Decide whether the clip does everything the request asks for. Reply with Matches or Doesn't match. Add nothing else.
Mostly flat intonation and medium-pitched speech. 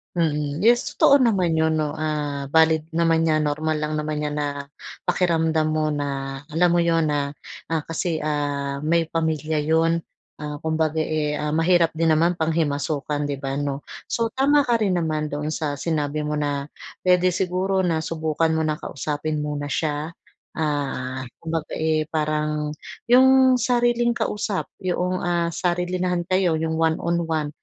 Matches